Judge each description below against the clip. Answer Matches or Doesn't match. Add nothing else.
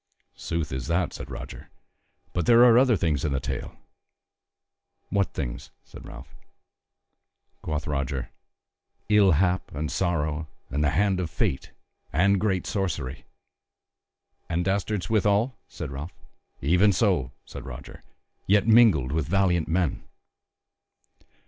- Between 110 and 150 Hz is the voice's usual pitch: Doesn't match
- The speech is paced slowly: Matches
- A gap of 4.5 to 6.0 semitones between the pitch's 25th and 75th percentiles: Matches